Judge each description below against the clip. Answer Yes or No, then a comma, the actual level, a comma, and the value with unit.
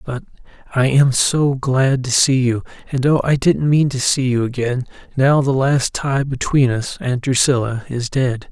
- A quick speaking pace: No, average, 175 wpm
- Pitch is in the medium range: No, low, 130 Hz